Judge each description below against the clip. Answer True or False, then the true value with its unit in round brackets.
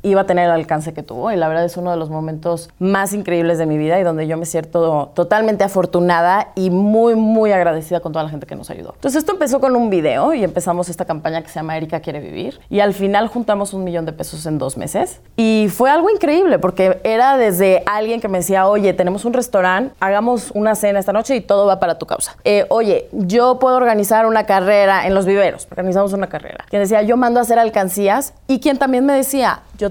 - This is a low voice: False (195 Hz)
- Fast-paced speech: True (235 wpm)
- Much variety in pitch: False (4.4 semitones)